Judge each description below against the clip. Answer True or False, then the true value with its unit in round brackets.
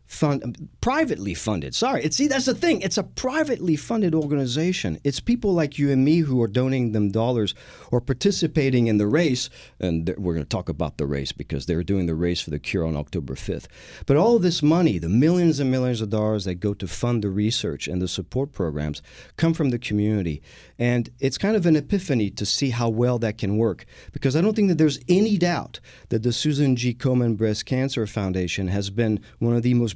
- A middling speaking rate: False (220 wpm)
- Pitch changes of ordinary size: False (7.5 semitones)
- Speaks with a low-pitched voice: True (120 Hz)